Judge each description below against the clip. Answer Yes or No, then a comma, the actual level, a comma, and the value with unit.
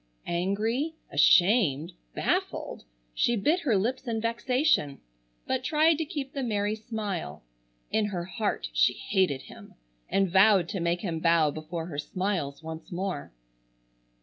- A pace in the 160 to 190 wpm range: No, average, 140 wpm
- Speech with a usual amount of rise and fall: No, wide, 5.7 semitones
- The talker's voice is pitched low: No, high, 195 Hz